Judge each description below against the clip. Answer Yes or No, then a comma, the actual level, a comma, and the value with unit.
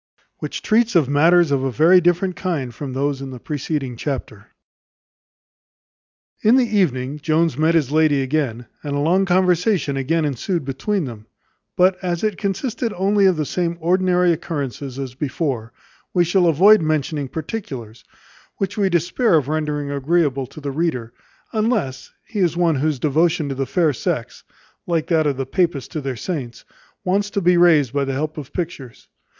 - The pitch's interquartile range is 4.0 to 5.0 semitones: Yes, average, 4.6 semitones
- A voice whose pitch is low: No, medium, 155 Hz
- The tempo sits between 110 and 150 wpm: No, average, 170 wpm